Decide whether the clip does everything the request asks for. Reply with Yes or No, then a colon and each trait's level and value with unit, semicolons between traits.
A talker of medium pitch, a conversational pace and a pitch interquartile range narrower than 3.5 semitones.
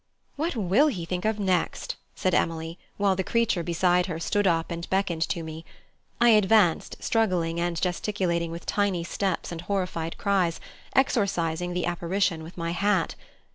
Yes: medium, 180 Hz; average, 160 wpm; average, 3.1 semitones